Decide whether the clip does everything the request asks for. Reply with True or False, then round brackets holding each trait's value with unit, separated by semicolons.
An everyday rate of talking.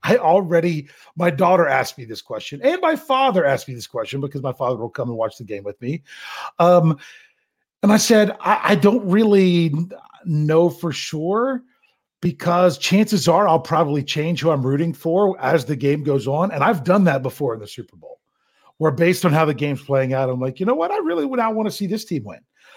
False (220 wpm)